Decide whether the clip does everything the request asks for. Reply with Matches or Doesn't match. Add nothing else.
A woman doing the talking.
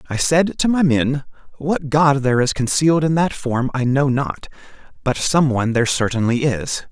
Doesn't match